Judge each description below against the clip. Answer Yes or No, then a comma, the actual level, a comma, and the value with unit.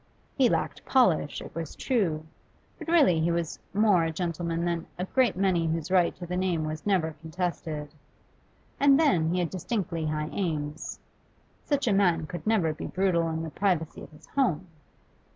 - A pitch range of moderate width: Yes, average, 3.4 semitones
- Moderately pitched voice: Yes, medium, 170 Hz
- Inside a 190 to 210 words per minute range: No, average, 175 wpm